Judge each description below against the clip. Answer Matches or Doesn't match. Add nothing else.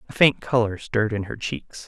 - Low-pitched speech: Matches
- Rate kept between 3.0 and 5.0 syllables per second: Doesn't match